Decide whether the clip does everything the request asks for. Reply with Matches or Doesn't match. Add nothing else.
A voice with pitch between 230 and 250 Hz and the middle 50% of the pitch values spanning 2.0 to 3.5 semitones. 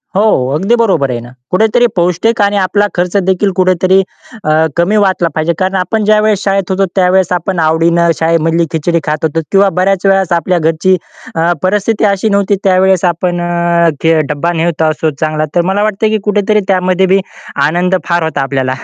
Doesn't match